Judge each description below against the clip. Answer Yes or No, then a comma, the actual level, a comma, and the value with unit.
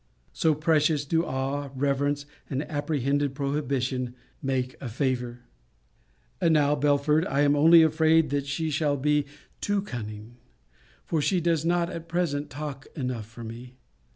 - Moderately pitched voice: Yes, medium, 145 Hz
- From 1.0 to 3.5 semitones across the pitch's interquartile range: Yes, average, 2.9 semitones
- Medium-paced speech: Yes, average, 145 wpm